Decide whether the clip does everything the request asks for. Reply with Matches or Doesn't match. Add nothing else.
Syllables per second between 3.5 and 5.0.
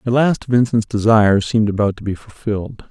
Doesn't match